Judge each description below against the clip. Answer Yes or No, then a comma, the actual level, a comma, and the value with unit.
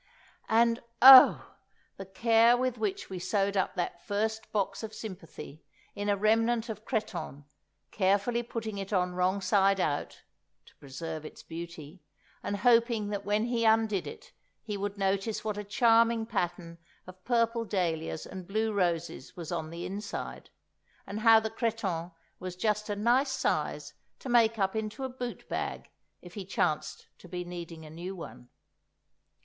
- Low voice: No, high, 200 Hz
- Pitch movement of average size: Yes, average, 3.9 semitones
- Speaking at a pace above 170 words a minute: No, average, 160 wpm